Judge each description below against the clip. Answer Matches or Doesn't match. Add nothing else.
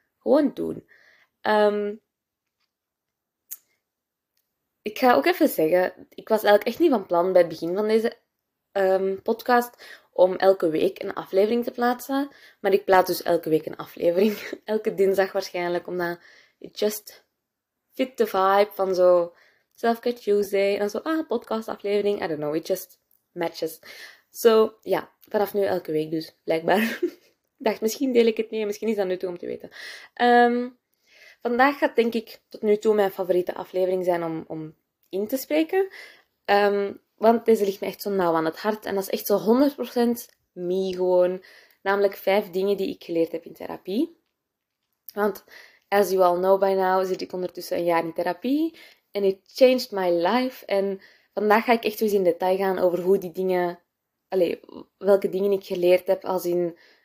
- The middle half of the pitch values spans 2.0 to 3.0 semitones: Doesn't match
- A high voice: Matches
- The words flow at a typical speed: Matches